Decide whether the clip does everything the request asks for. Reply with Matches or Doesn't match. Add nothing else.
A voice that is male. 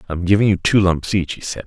Matches